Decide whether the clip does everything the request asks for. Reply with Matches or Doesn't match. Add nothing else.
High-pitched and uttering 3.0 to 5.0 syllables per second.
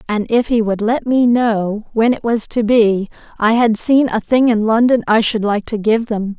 Matches